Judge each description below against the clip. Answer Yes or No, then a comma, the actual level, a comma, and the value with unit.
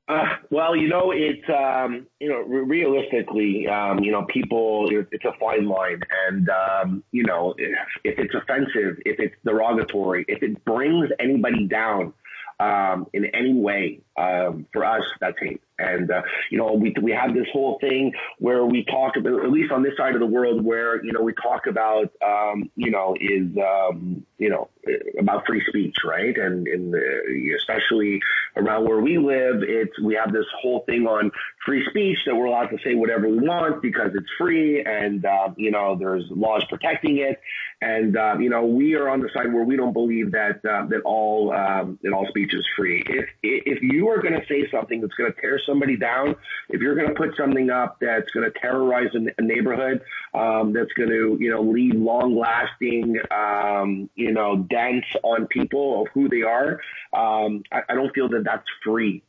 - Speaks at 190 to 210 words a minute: Yes, average, 195 wpm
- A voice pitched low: Yes, low, 115 Hz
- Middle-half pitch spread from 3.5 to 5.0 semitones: Yes, average, 3.9 semitones